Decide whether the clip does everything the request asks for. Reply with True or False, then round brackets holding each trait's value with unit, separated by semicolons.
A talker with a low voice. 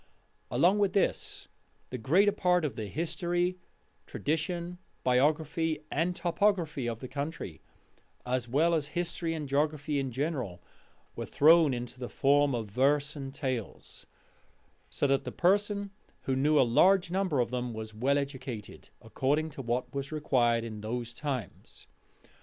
False (145 Hz)